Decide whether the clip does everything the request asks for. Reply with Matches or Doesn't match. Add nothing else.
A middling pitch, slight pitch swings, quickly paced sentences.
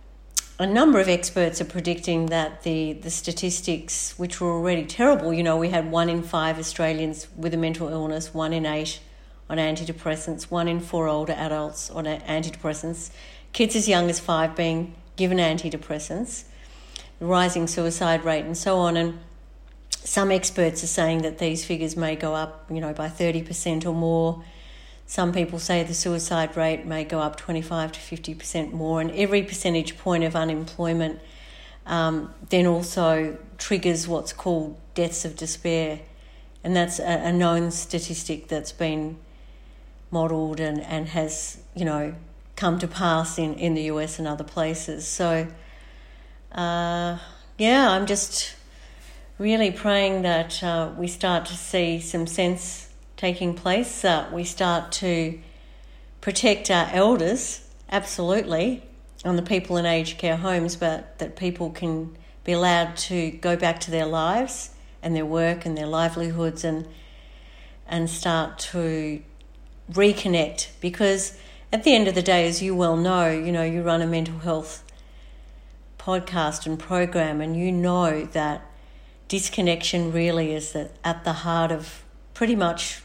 Doesn't match